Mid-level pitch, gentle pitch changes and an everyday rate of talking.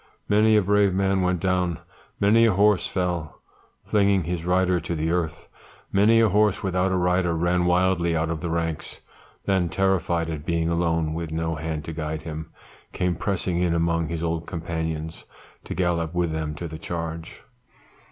No: very low, 85 Hz; narrow, 2.3 semitones; average, 175 wpm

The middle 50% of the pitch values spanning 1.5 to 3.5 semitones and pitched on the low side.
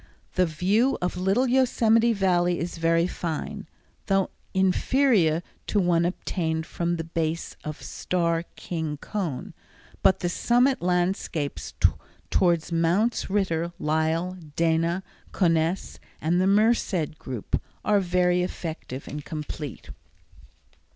No: average, 2.9 semitones; medium, 175 Hz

